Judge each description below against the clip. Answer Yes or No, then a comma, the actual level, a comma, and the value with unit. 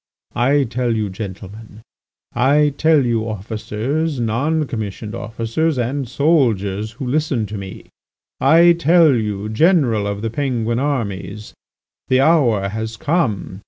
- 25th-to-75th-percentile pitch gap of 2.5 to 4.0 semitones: No, average, 5.2 semitones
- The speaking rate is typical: No, slow, 125 wpm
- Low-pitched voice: Yes, low, 115 Hz